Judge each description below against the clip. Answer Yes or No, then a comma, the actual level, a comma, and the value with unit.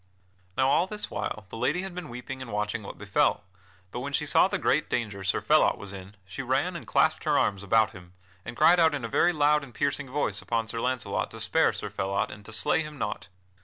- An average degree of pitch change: No, wide, 6.1 semitones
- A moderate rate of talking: No, fast, 240 wpm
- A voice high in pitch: No, low, 115 Hz